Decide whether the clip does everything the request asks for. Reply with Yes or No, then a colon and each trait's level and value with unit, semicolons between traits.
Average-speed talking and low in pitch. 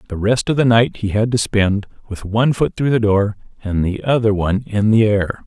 No: fast, 240 wpm; low, 110 Hz